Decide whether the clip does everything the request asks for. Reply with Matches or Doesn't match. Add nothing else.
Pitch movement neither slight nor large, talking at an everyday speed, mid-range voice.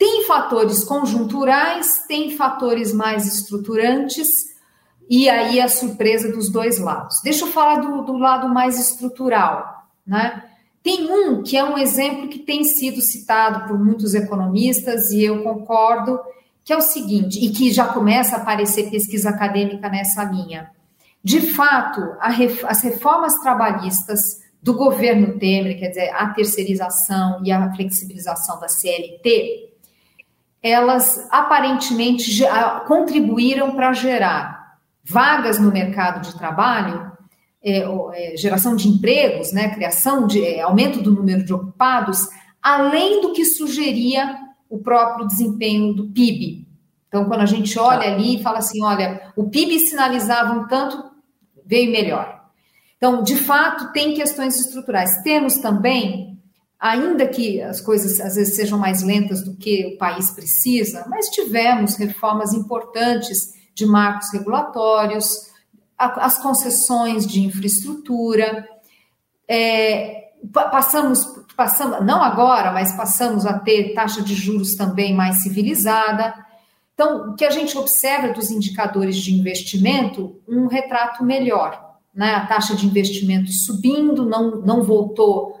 Doesn't match